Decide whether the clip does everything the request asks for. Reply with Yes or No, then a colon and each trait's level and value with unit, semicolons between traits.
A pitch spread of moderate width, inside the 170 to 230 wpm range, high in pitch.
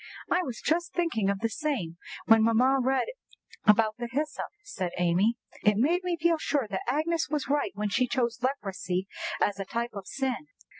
No: wide, 6.4 semitones; average, 185 wpm; high, 240 Hz